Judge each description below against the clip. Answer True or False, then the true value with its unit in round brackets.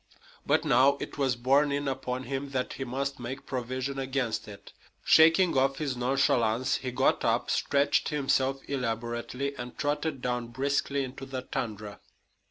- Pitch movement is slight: True (2.0 semitones)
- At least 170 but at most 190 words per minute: False (155 wpm)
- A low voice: True (130 Hz)